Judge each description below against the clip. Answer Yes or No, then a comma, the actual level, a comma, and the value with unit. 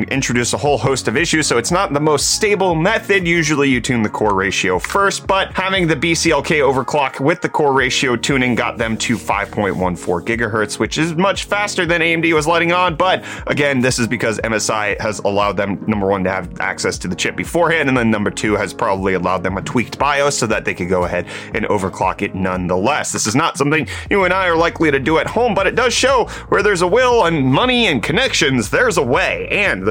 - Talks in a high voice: No, low, 135 Hz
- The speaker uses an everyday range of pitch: No, wide, 8.1 semitones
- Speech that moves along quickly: Yes, fast, 225 wpm